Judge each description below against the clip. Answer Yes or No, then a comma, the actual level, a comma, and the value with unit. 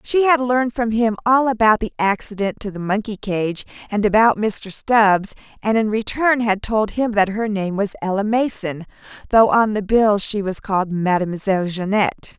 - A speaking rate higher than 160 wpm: Yes, average, 185 wpm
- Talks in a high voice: Yes, high, 210 Hz